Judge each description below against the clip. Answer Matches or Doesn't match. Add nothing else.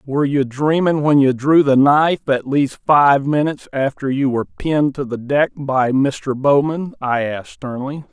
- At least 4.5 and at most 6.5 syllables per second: Matches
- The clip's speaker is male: Matches